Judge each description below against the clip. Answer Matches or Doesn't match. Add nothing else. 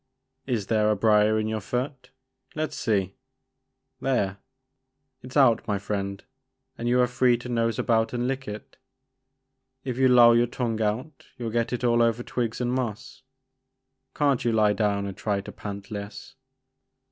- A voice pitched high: Doesn't match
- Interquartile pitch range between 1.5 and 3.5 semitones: Matches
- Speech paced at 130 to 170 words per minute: Doesn't match